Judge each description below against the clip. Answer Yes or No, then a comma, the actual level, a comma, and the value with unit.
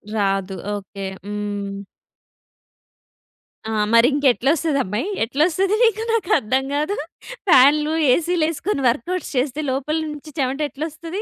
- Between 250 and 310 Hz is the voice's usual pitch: Yes, very high, 280 Hz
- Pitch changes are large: Yes, wide, 6.0 semitones